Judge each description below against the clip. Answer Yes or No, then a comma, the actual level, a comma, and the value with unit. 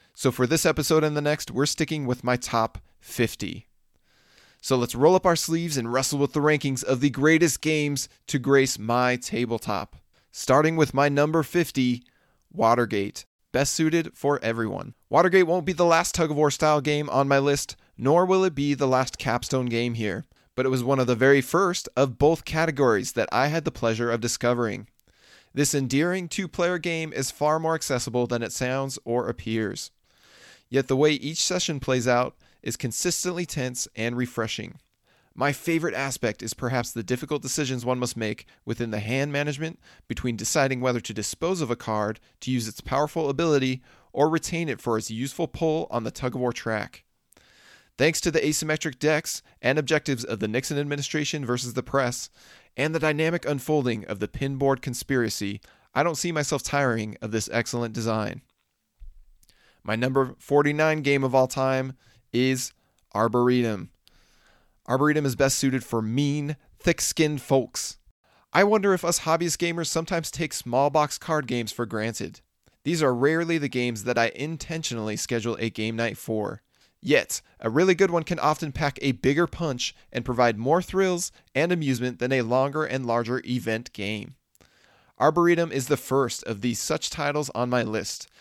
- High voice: No, low, 135 Hz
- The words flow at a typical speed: Yes, average, 175 wpm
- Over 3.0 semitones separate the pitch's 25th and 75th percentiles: Yes, average, 4.3 semitones